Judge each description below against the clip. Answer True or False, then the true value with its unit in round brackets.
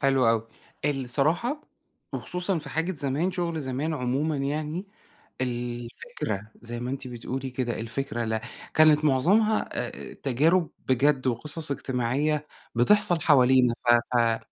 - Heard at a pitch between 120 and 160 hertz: True (135 Hz)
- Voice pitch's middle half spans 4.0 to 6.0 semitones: True (4.4 semitones)